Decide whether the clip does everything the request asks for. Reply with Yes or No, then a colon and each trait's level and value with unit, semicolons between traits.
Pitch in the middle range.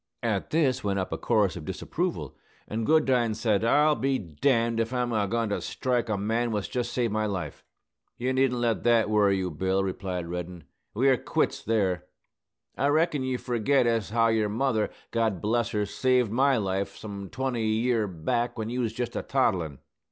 No: low, 115 Hz